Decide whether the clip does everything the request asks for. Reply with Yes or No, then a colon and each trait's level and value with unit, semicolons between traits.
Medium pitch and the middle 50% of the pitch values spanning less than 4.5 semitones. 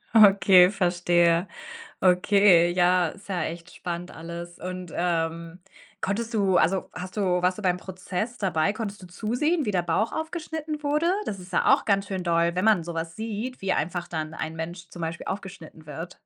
Yes: medium, 180 Hz; average, 2.9 semitones